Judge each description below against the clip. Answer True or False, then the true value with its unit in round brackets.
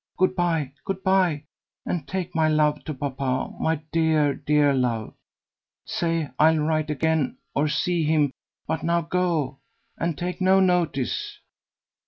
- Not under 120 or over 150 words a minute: True (140 wpm)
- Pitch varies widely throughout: False (2.8 semitones)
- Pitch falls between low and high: True (160 Hz)